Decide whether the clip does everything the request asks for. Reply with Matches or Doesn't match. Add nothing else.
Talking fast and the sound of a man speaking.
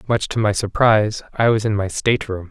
Matches